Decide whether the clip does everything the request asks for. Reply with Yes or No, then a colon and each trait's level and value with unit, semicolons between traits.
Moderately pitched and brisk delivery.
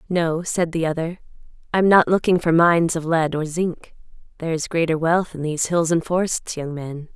Yes: medium, 165 Hz; fast, 210 wpm